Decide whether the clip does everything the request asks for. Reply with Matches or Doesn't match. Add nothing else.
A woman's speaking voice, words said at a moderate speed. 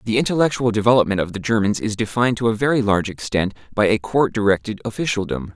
Doesn't match